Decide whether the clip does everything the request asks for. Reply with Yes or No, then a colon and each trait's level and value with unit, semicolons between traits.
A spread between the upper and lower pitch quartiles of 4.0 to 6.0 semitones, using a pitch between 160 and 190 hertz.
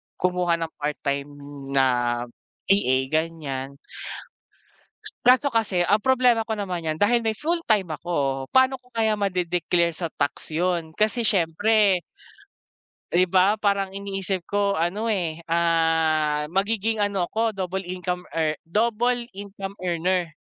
Yes: average, 4.4 semitones; medium, 185 Hz